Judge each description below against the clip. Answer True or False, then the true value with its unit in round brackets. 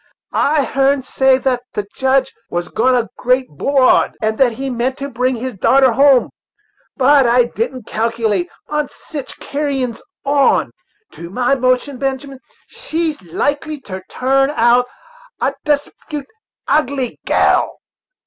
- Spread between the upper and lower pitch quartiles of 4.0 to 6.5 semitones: False (2.5 semitones)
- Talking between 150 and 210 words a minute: False (135 wpm)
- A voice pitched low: False (260 Hz)